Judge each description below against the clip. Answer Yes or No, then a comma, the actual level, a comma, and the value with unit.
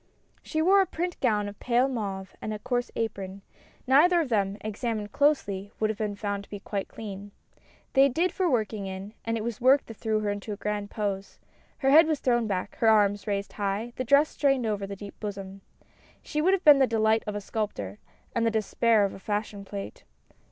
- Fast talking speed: Yes, fast, 215 wpm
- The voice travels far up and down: No, average, 3.9 semitones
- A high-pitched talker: Yes, high, 215 Hz